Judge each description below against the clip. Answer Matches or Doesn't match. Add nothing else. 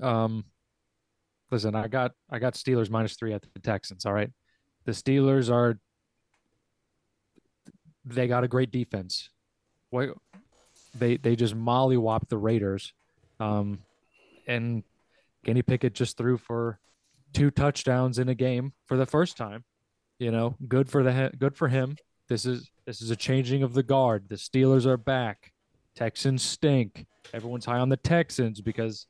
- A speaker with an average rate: Matches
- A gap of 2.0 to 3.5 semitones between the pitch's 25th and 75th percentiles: Matches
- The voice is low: Matches